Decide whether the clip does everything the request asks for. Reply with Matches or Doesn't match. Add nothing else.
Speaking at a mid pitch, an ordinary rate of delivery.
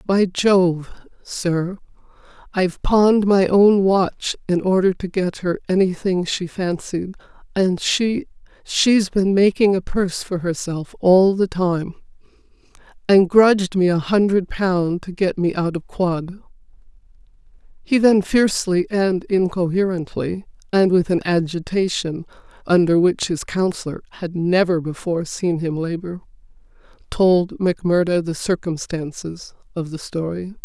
Doesn't match